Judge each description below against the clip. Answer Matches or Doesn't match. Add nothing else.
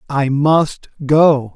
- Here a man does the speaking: Matches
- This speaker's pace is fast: Doesn't match